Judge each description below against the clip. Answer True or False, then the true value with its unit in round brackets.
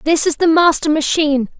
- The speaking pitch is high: True (310 Hz)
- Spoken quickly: False (190 wpm)